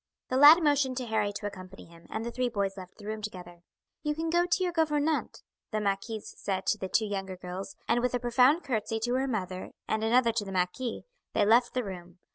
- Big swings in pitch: No, average, 4.8 semitones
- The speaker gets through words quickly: Yes, fast, 225 wpm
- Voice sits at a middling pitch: No, high, 220 Hz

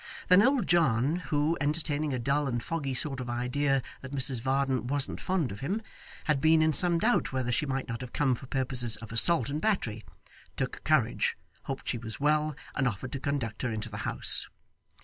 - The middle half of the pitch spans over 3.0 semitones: Yes, average, 3.7 semitones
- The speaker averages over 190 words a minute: Yes, average, 200 wpm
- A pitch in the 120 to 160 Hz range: Yes, low, 135 Hz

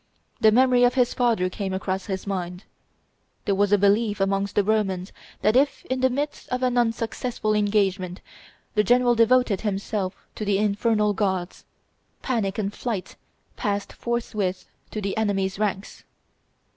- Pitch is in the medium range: No, high, 210 Hz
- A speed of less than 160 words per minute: Yes, average, 150 wpm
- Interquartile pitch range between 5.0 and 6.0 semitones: No, average, 3.4 semitones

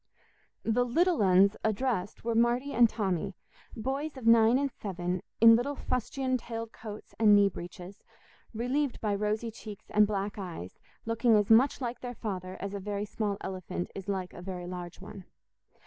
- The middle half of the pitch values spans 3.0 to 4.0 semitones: Yes, average, 3.6 semitones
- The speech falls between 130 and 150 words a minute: No, average, 170 wpm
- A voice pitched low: No, high, 215 Hz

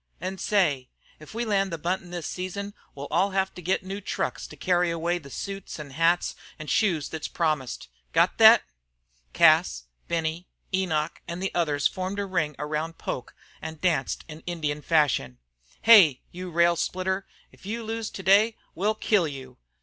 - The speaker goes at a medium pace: Yes, average, 170 wpm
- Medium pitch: Yes, medium, 175 Hz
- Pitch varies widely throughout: No, average, 3.8 semitones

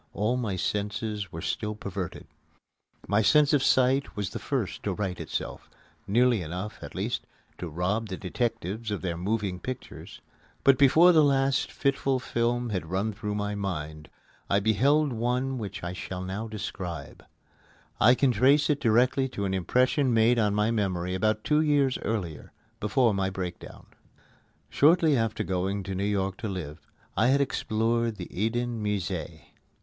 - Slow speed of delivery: No, average, 160 wpm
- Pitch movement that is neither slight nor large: Yes, average, 4.8 semitones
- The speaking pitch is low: Yes, low, 110 Hz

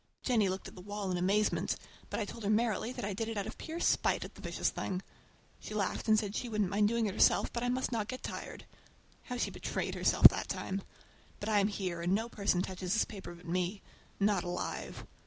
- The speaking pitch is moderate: No, high, 205 Hz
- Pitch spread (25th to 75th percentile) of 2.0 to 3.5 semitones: Yes, average, 2.9 semitones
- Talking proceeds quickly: Yes, fast, 230 wpm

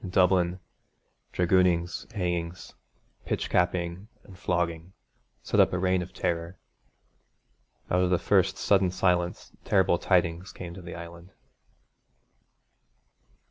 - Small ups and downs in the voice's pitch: Yes, narrow, 1.3 semitones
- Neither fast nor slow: No, slow, 115 wpm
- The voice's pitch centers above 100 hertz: No, very low, 90 Hz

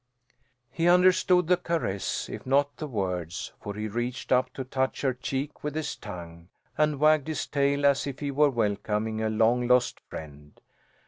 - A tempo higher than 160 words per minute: Yes, average, 175 wpm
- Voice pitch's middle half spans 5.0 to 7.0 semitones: Yes, wide, 5.6 semitones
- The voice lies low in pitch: Yes, low, 130 Hz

